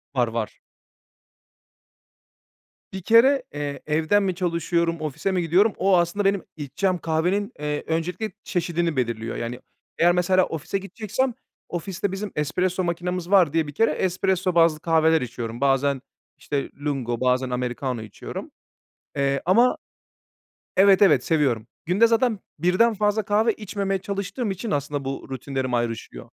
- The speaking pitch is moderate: Yes, medium, 170 Hz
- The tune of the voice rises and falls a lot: Yes, wide, 5.7 semitones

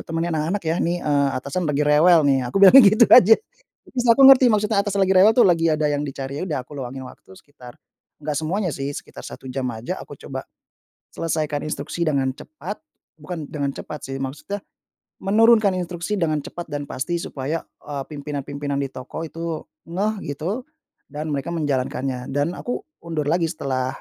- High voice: No, medium, 155 Hz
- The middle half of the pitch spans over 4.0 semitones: Yes, average, 4.4 semitones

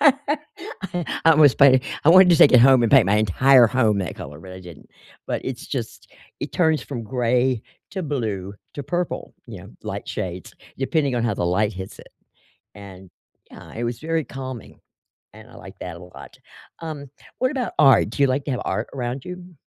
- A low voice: Yes, low, 130 Hz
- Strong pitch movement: Yes, wide, 6.4 semitones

